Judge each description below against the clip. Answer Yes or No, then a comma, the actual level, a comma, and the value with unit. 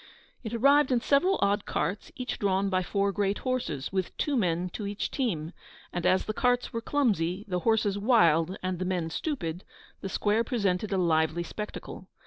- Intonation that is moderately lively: Yes, average, 4.4 semitones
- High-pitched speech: Yes, high, 200 Hz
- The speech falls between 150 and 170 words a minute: No, average, 180 wpm